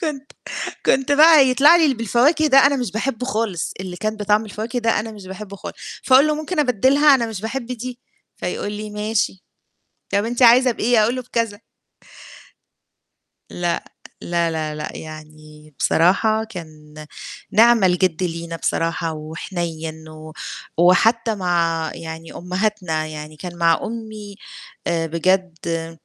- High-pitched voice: Yes, high, 205 Hz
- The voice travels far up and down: Yes, wide, 6.2 semitones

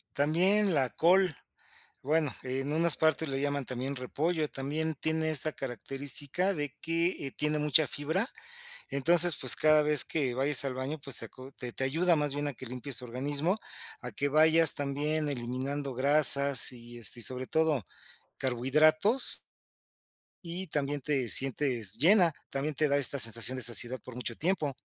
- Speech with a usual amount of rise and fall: Yes, average, 3.3 semitones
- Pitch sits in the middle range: Yes, medium, 145 Hz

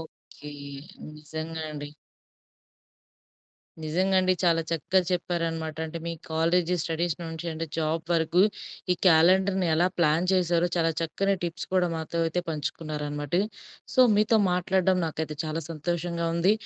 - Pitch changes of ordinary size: No, narrow, 2.0 semitones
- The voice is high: No, medium, 165 Hz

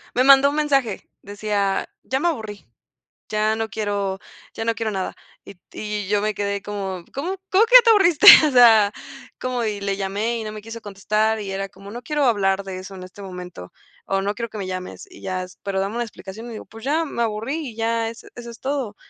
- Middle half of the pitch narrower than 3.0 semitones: No, average, 3.3 semitones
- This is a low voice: No, high, 215 Hz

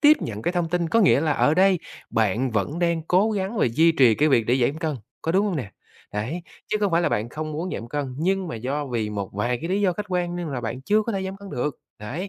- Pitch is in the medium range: Yes, medium, 160 Hz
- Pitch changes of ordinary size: No, wide, 6.9 semitones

